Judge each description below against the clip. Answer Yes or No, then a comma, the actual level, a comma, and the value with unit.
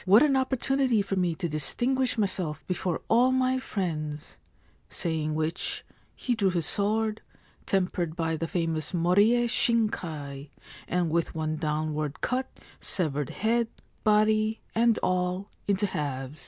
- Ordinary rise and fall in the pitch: No, wide, 5.9 semitones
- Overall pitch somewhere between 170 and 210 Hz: Yes, medium, 185 Hz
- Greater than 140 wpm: No, slow, 135 wpm